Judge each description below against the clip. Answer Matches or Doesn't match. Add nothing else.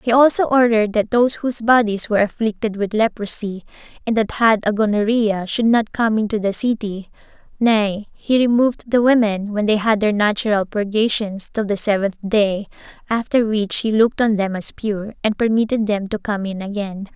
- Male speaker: Doesn't match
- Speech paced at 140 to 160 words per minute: Doesn't match